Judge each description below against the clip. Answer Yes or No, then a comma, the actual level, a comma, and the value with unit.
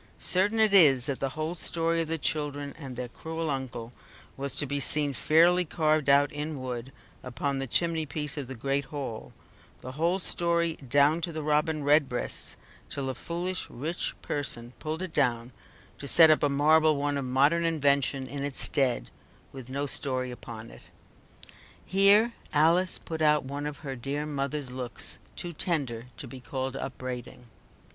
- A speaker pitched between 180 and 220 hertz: No, medium, 145 Hz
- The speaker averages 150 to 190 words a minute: Yes, average, 170 wpm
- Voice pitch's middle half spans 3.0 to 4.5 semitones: Yes, average, 3.4 semitones